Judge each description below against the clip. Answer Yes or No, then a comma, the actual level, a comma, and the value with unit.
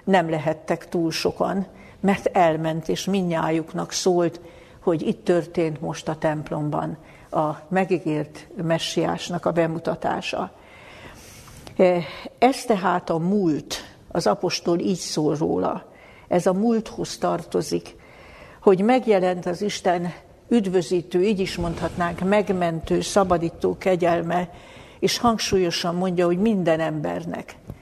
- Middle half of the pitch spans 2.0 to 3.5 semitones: Yes, average, 2.8 semitones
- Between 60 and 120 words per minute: Yes, average, 110 wpm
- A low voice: No, medium, 175 Hz